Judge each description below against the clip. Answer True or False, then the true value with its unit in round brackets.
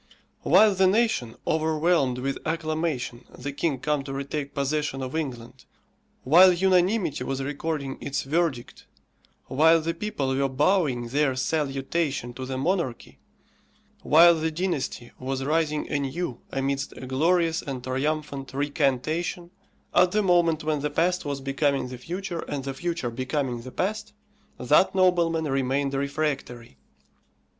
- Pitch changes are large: False (3.8 semitones)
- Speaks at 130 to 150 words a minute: True (135 wpm)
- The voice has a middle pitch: True (145 Hz)